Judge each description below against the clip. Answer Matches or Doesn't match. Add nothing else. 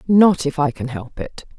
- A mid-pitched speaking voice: Matches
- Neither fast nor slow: Doesn't match